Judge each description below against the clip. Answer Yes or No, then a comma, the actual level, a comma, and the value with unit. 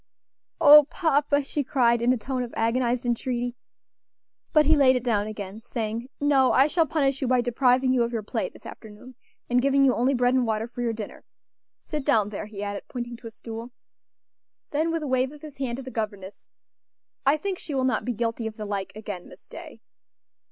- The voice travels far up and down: No, average, 3.4 semitones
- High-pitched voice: Yes, high, 245 Hz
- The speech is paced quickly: Yes, fast, 210 wpm